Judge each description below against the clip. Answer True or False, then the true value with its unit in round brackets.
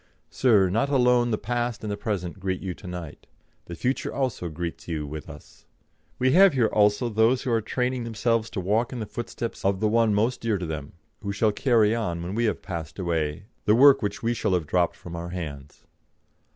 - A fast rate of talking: True (215 wpm)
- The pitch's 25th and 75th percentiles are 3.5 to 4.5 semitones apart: False (5.2 semitones)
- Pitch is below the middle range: True (105 Hz)